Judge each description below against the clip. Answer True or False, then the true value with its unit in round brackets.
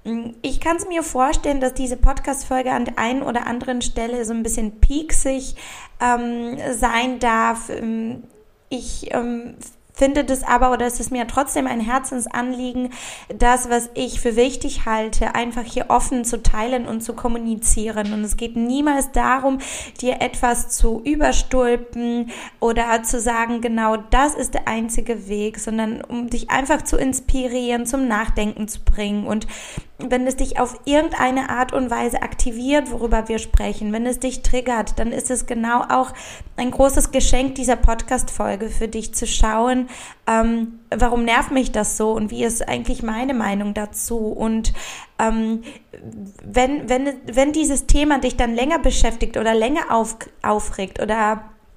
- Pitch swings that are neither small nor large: False (2.2 semitones)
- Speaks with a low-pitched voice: False (240 Hz)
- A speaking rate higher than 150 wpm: True (160 wpm)